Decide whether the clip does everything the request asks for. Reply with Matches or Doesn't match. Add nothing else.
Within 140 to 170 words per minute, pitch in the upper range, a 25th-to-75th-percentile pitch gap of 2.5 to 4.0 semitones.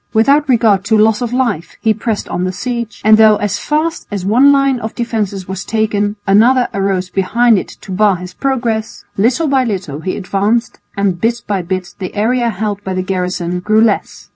Doesn't match